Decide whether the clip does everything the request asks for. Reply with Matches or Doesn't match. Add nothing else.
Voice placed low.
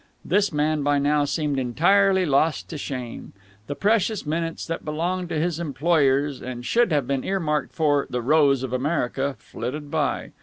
Doesn't match